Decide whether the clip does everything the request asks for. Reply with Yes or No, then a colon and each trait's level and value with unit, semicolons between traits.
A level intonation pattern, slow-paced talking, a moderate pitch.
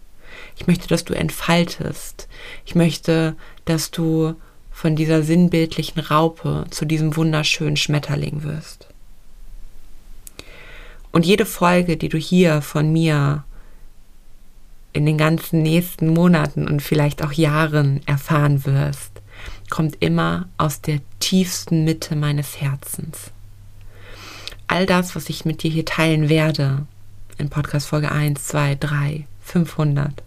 Yes: narrow, 2.2 semitones; slow, 120 wpm; medium, 155 Hz